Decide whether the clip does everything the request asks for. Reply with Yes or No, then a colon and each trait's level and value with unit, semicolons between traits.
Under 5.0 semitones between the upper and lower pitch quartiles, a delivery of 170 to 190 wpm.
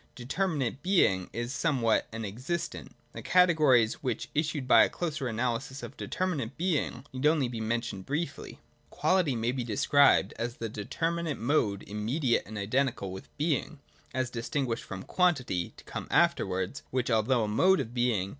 No: average, 5.3 semitones; average, 185 wpm